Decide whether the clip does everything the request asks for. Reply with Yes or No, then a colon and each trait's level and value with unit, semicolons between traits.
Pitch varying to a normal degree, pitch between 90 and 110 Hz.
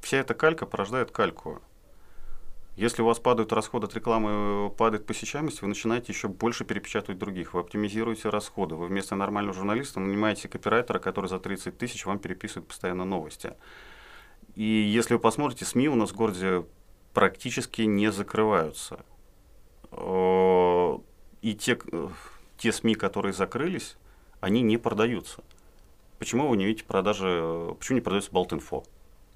Yes: average, 3.1 semitones; low, 105 Hz